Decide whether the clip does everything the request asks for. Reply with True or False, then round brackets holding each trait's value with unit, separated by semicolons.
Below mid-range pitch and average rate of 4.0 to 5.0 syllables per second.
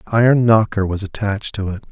False (105 Hz; 6.3 syllables/s)